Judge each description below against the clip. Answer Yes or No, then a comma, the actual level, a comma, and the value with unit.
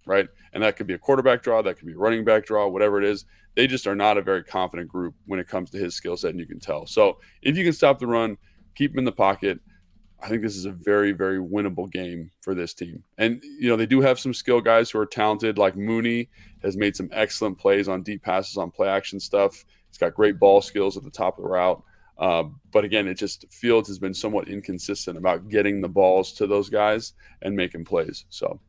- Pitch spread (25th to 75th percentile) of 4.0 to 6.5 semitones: No, average, 2.9 semitones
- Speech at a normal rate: No, fast, 250 wpm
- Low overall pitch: Yes, low, 100 Hz